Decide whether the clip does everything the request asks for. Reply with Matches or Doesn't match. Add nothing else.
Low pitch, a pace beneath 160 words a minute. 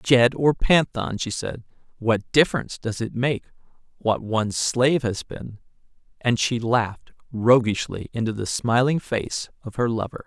Matches